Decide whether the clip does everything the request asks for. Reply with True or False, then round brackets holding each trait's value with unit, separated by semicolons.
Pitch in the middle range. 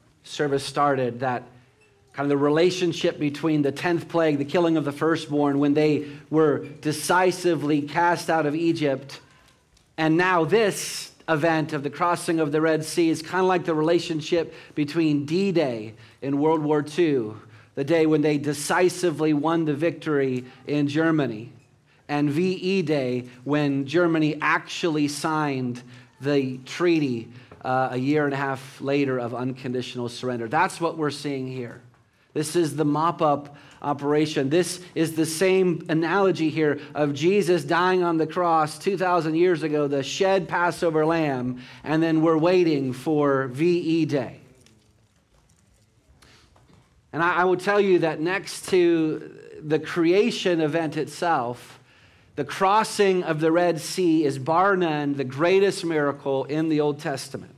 True (155 Hz)